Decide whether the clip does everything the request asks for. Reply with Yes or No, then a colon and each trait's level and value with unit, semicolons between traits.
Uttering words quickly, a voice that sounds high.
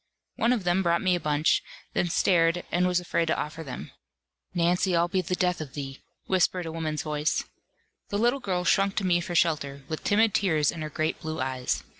No: fast, 210 wpm; medium, 170 Hz